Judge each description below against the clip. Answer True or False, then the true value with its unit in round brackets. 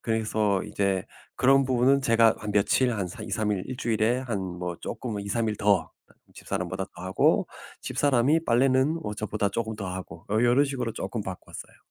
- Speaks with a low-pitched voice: True (110 Hz)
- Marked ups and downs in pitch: False (3.8 semitones)